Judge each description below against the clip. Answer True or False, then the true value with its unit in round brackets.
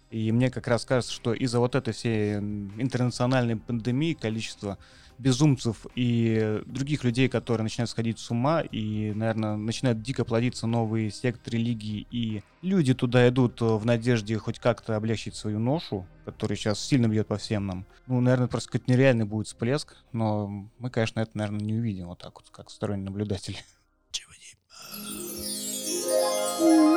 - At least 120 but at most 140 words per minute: False (150 wpm)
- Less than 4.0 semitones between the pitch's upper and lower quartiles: True (2.7 semitones)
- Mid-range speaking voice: False (115 Hz)